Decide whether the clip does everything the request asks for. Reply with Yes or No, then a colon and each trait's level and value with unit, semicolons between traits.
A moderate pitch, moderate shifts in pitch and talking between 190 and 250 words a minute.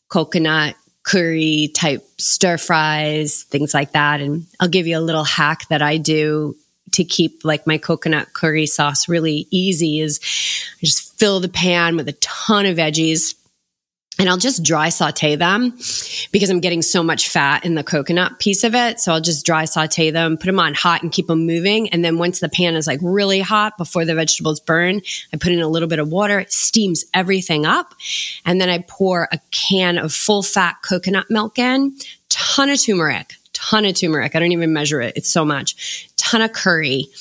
Yes: medium, 170 Hz; average, 3.4 semitones; average, 200 wpm